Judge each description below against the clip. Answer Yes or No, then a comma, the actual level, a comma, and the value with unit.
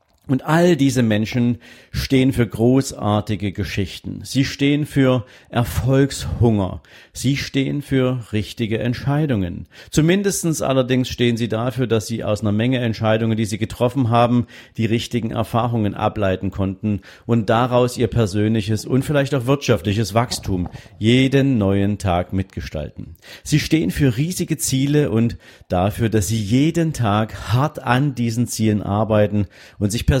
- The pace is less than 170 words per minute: Yes, average, 135 wpm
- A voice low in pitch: Yes, low, 115 Hz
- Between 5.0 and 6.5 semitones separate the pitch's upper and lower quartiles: No, average, 4.0 semitones